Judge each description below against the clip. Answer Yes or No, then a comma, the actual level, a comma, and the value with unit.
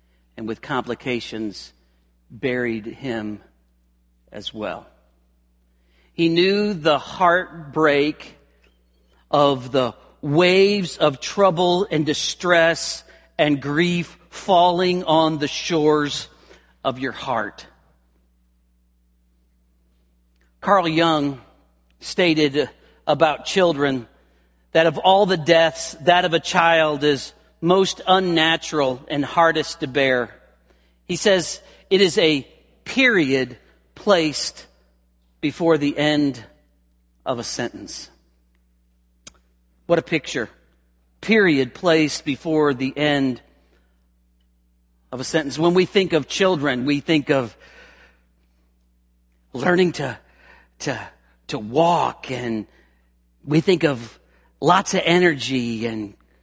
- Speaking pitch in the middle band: No, low, 130 Hz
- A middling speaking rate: No, slow, 100 wpm